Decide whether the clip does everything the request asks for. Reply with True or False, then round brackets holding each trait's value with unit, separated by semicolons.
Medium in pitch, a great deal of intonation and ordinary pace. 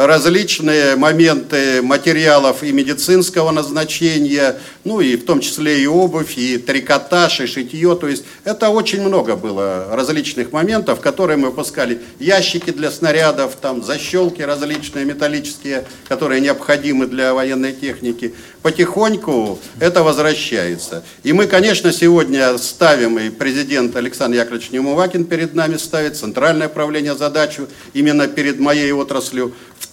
False (145 Hz; 3.5 semitones; 130 wpm)